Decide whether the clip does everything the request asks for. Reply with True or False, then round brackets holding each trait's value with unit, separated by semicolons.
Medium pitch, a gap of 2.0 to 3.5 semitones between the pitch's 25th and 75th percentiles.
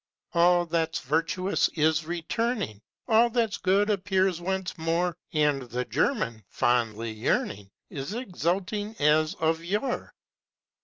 False (170 Hz; 4.8 semitones)